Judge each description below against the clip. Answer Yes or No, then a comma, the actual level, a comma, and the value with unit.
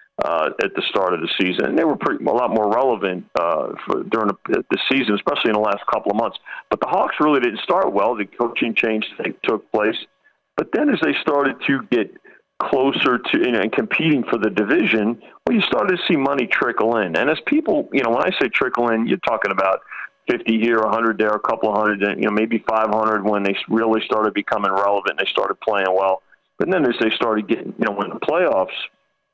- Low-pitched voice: Yes, low, 110 Hz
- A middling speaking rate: No, fast, 235 wpm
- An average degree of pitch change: No, narrow, 1.4 semitones